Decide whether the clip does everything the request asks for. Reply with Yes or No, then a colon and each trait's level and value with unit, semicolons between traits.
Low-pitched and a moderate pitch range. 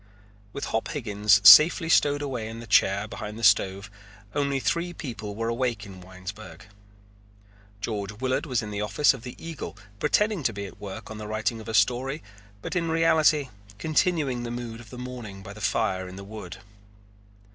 Yes: low, 115 Hz; average, 5.0 semitones